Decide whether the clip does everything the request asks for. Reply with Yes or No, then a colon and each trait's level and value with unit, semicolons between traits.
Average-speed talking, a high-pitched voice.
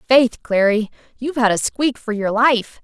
Yes: average, 190 wpm; high, 230 Hz